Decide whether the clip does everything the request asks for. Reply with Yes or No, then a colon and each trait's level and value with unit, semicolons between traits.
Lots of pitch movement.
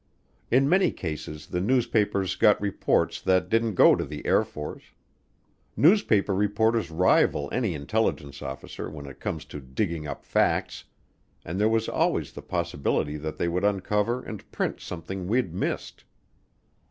Yes: wide, 6.3 semitones